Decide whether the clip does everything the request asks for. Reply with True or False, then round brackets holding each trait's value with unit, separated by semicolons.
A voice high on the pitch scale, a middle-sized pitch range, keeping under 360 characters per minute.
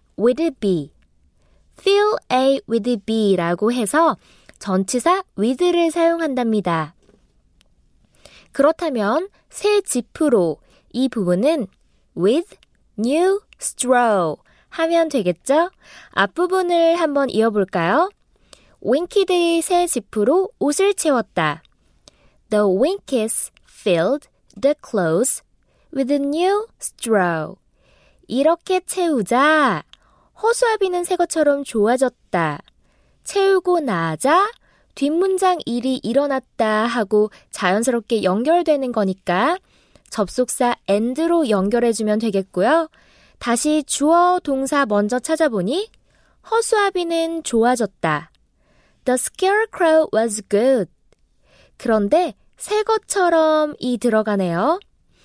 False (275 Hz; 7.5 semitones; 265 characters per minute)